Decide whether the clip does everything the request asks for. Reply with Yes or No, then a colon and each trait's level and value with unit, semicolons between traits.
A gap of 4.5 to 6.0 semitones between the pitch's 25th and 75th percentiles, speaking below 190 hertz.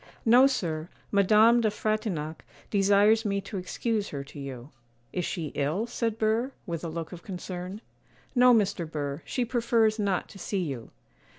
No: average, 5.2 semitones; high, 200 Hz